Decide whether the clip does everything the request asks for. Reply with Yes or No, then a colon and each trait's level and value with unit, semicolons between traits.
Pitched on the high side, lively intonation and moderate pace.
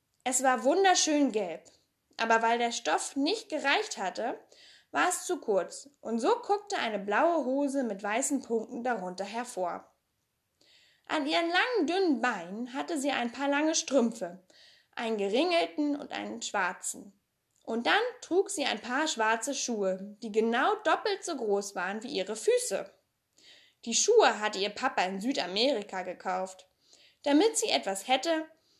Yes: very high, 270 Hz; wide, 6.6 semitones; average, 150 wpm